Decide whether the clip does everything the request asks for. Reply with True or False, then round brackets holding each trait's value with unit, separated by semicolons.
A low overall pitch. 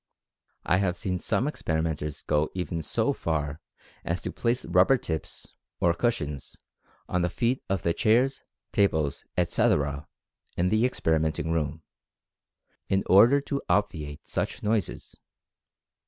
True (85 Hz)